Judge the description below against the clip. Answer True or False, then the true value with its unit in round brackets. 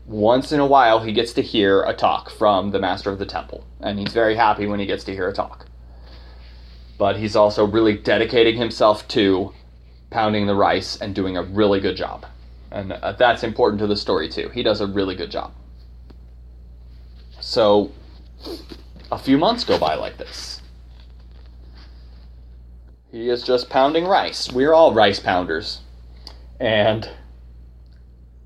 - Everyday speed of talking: True (155 wpm)